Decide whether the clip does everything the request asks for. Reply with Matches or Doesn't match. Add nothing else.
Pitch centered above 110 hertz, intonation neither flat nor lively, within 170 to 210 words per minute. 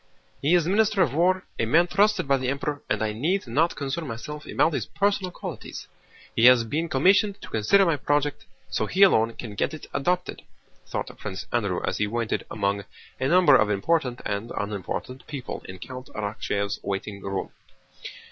Doesn't match